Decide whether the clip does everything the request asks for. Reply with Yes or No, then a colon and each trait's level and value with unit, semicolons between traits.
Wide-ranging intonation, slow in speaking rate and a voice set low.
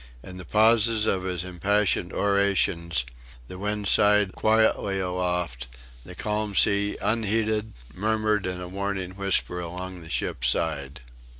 No: average, 2.7 semitones; slow, 130 wpm; low, 100 Hz